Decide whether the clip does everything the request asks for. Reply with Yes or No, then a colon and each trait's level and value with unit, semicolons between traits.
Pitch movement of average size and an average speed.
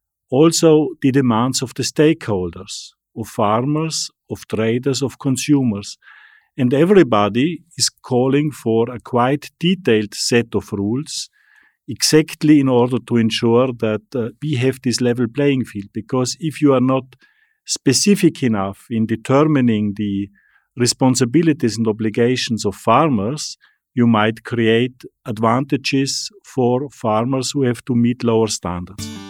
No: average, 4.3 semitones; slow, 130 wpm